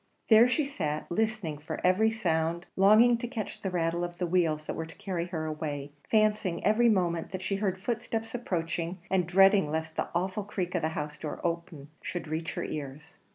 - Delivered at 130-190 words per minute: No, average, 200 wpm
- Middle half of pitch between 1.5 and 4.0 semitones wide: No, average, 4.5 semitones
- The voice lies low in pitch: No, medium, 180 Hz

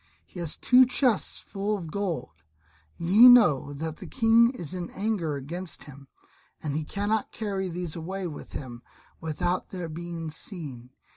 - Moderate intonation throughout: Yes, average, 4.7 semitones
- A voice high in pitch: No, medium, 175 Hz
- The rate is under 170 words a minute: Yes, average, 155 wpm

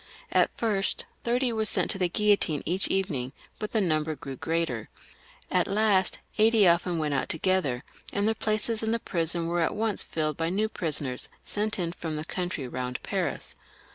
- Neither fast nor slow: Yes, average, 180 wpm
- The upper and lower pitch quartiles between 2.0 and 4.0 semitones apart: No, wide, 5.4 semitones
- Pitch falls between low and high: Yes, medium, 180 Hz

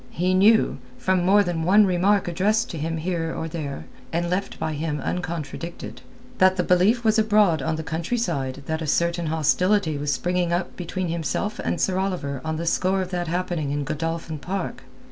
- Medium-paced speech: Yes, average, 175 wpm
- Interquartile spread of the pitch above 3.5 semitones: No, average, 3.0 semitones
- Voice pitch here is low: No, medium, 175 Hz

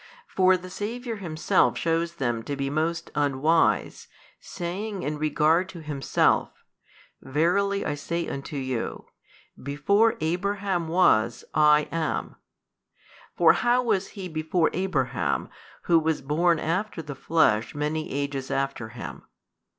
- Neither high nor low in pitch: Yes, medium, 160 Hz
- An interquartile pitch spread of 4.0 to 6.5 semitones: Yes, average, 4.4 semitones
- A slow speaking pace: Yes, slow, 125 wpm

